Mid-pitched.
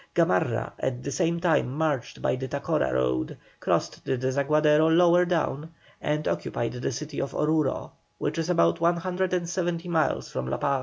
Yes: medium, 150 Hz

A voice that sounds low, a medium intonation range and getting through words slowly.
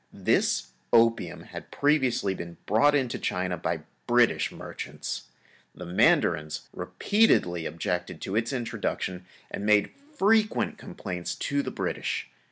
No: low, 105 Hz; wide, 7.9 semitones; slow, 120 wpm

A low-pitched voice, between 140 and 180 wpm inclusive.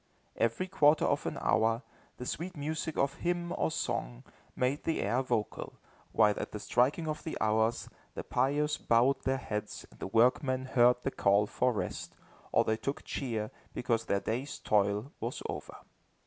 Yes: low, 125 Hz; average, 170 wpm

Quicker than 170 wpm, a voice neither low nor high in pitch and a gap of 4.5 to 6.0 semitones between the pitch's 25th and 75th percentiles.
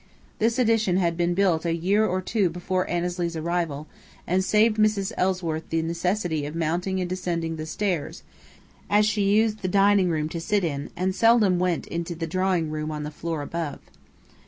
No: average, 180 wpm; medium, 180 Hz; average, 3.2 semitones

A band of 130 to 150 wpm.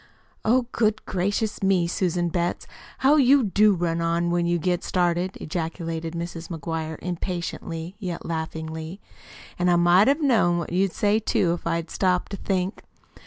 No: average, 160 wpm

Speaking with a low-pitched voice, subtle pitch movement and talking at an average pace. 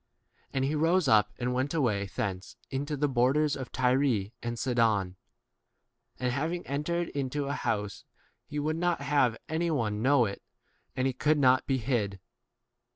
No: low, 130 Hz; average, 4.2 semitones; average, 170 wpm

